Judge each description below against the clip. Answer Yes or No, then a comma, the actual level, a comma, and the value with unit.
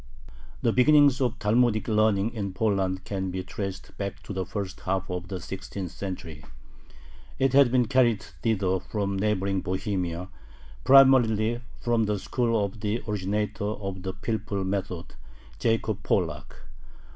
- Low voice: Yes, low, 100 Hz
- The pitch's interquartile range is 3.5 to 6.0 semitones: No, average, 3.1 semitones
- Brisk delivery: No, average, 140 wpm